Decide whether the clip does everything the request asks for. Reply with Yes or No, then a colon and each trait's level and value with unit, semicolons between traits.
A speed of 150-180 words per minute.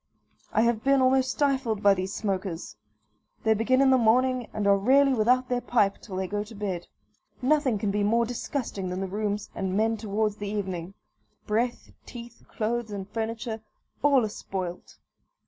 Yes: average, 175 wpm